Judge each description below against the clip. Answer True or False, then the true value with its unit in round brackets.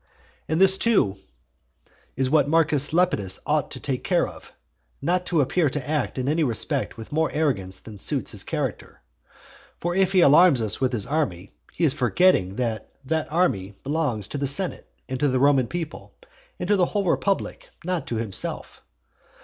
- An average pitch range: False (6.5 semitones)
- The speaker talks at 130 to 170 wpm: False (180 wpm)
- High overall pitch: False (145 Hz)